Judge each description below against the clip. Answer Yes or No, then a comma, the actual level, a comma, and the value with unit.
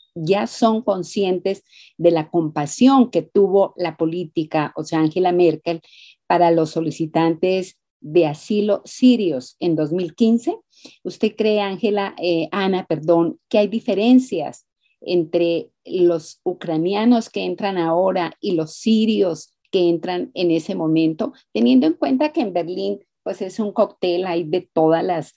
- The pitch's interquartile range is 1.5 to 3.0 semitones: No, average, 3.9 semitones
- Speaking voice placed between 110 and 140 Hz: No, medium, 180 Hz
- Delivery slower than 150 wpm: Yes, average, 140 wpm